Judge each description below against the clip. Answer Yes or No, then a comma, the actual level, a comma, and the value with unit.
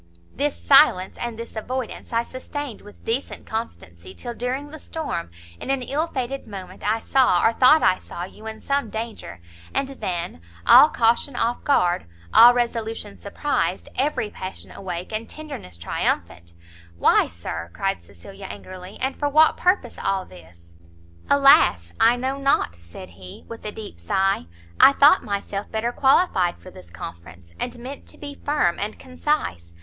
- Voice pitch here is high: Yes, high, 220 Hz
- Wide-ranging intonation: Yes, wide, 7.4 semitones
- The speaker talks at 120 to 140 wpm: No, average, 165 wpm